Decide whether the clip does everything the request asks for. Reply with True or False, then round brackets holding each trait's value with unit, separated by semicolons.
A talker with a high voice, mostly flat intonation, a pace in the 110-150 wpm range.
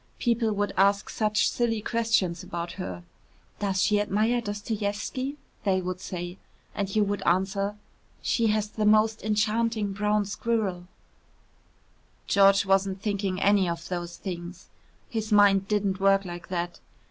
True (200 Hz; 2.2 semitones; 140 wpm)